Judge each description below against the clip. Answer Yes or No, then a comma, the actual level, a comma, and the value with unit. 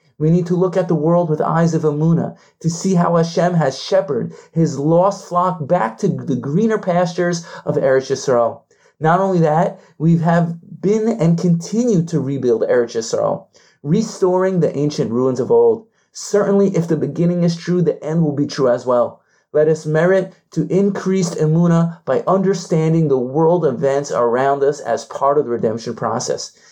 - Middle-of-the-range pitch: Yes, medium, 170 Hz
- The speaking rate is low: No, average, 175 wpm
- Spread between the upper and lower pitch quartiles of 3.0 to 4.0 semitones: Yes, average, 3.7 semitones